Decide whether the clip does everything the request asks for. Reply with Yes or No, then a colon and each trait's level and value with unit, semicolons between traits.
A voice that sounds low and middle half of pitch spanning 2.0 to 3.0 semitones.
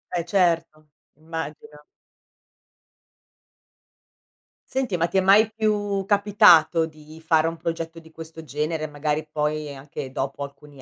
No: medium, 160 Hz; narrow, 2.6 semitones